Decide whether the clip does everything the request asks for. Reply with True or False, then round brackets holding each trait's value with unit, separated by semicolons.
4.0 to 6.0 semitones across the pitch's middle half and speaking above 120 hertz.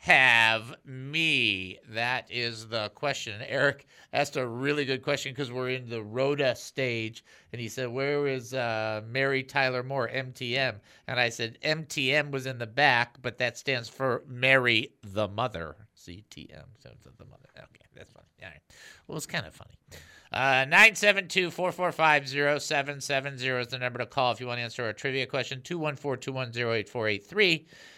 False (3.1 semitones; 130 Hz)